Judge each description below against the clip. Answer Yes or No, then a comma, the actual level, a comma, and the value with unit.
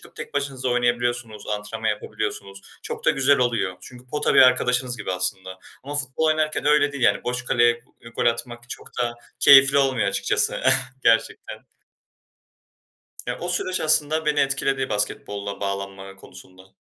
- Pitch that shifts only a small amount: No, average, 4.8 semitones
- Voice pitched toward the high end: No, low, 125 Hz